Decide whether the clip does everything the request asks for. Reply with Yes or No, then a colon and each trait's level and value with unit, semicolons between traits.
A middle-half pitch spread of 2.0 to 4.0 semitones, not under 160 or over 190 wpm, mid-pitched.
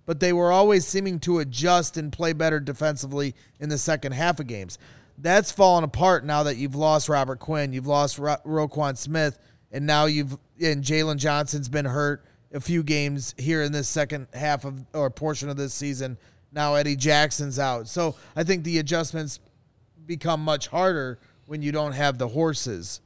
Yes: narrow, 2.4 semitones; average, 180 wpm; medium, 150 Hz